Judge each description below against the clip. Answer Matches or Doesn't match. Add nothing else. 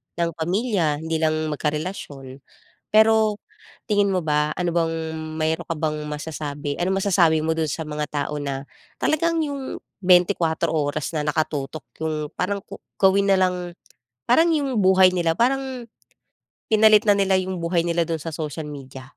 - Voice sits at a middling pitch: Matches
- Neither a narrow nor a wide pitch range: Matches